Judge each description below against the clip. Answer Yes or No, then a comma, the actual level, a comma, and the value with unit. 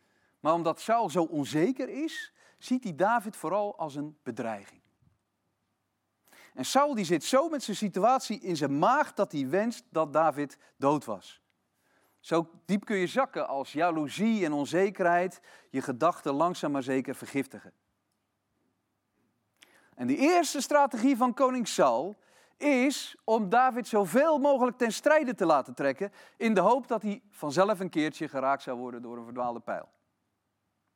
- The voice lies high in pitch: No, medium, 175 Hz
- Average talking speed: Yes, average, 150 wpm